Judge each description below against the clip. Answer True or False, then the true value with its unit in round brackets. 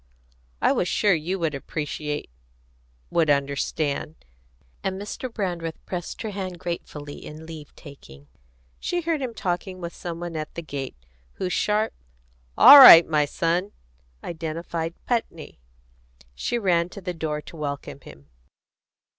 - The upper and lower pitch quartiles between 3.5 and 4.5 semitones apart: True (3.8 semitones)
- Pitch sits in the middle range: True (170 Hz)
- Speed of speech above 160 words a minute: False (140 wpm)